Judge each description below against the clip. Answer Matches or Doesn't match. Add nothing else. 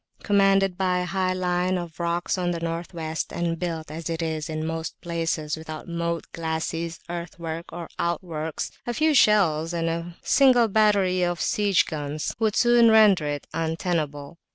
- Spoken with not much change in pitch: Matches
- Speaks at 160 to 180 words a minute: Matches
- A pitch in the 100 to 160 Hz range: Doesn't match